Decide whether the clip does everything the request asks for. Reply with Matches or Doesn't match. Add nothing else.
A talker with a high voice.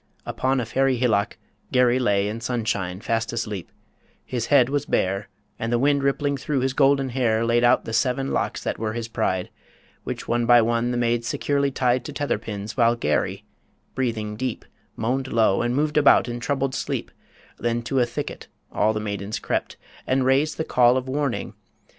Doesn't match